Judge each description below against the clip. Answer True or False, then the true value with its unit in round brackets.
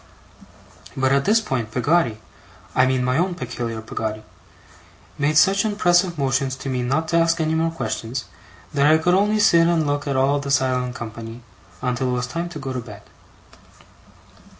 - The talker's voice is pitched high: False (140 Hz)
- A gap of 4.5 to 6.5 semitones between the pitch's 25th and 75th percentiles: True (4.9 semitones)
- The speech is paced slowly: False (175 wpm)